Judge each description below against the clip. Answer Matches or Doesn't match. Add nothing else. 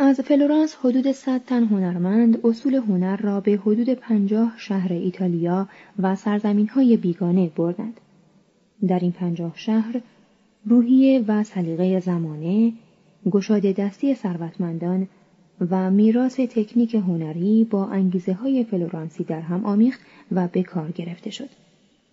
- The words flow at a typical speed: Matches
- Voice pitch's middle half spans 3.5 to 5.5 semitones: Matches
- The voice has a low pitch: Doesn't match